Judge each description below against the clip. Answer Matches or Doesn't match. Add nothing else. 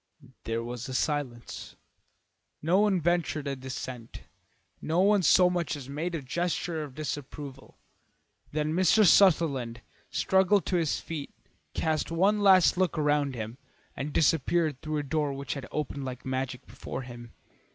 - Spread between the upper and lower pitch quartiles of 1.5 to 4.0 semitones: Doesn't match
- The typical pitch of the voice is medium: Matches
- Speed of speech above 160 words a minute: Doesn't match